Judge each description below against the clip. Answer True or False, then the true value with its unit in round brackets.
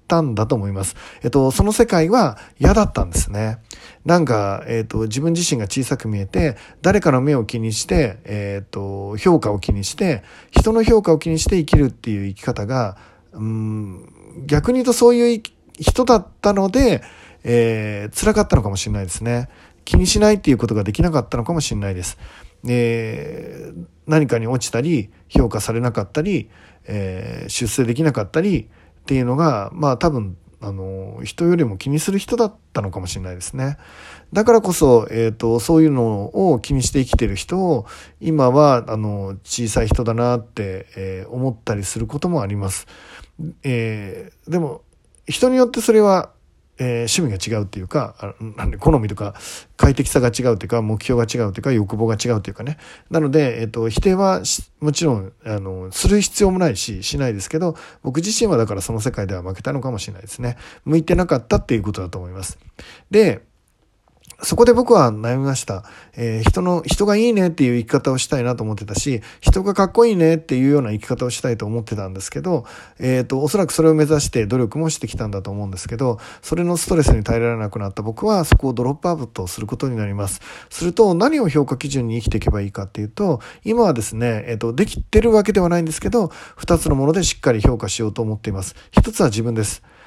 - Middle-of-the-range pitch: False (120 Hz)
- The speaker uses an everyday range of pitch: False (7.2 semitones)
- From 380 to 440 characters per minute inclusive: True (400 characters per minute)